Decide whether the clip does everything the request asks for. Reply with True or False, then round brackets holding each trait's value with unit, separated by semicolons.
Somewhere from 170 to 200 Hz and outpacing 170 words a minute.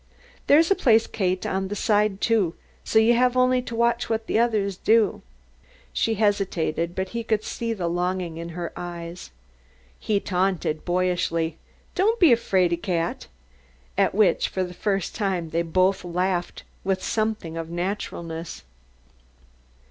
False (190 Hz; 150 wpm)